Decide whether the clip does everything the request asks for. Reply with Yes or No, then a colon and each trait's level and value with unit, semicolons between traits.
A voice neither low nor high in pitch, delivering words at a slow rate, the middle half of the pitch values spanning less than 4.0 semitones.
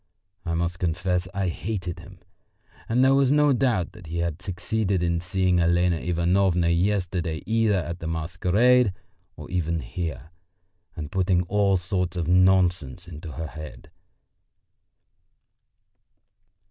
No: very low, 90 Hz; slow, 130 wpm; narrow, 2.4 semitones